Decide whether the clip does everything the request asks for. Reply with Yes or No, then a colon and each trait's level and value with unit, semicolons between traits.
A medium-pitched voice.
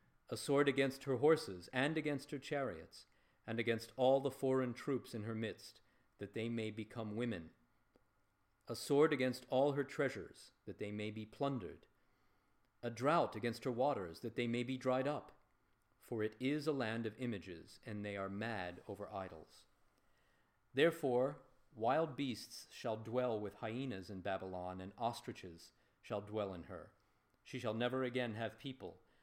No: low, 120 Hz